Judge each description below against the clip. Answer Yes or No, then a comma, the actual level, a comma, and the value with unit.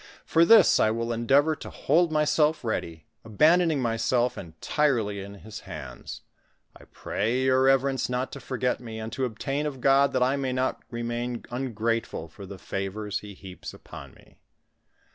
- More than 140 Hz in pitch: No, low, 120 Hz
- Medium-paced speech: Yes, average, 165 wpm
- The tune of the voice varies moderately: Yes, average, 4.0 semitones